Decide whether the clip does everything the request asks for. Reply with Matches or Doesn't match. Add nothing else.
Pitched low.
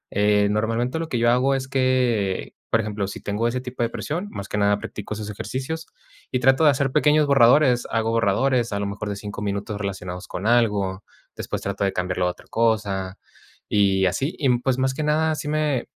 Matches